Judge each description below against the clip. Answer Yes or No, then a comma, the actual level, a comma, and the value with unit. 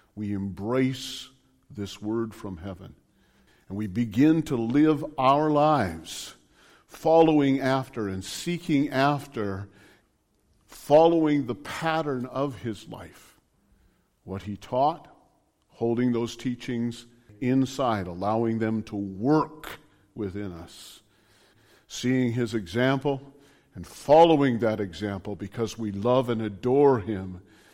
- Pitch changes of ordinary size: Yes, average, 5.0 semitones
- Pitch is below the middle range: Yes, low, 120 Hz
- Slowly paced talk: Yes, slow, 110 wpm